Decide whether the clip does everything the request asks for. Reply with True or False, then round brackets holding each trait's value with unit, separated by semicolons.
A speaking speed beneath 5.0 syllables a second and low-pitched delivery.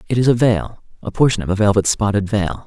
False (6.1 syllables/s; 105 Hz)